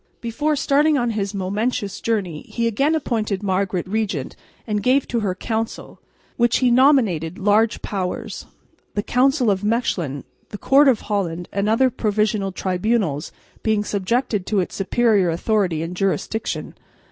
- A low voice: No, high, 210 Hz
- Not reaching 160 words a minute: Yes, average, 145 wpm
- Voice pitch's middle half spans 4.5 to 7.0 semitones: No, average, 3.9 semitones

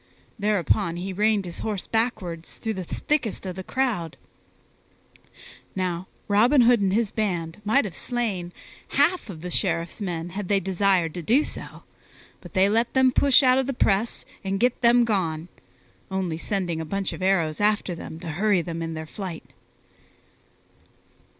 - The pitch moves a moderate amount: Yes, average, 4.3 semitones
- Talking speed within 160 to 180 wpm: Yes, average, 165 wpm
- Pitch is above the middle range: Yes, high, 195 Hz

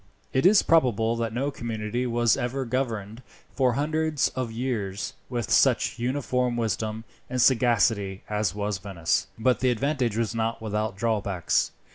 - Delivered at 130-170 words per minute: Yes, average, 145 wpm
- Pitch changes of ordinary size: Yes, average, 3.1 semitones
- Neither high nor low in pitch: No, low, 115 Hz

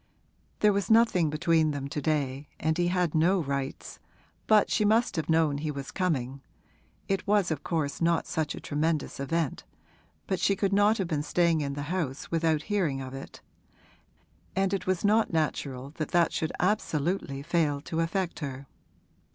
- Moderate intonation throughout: Yes, average, 4.4 semitones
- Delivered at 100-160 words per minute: No, average, 175 wpm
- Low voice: No, medium, 160 Hz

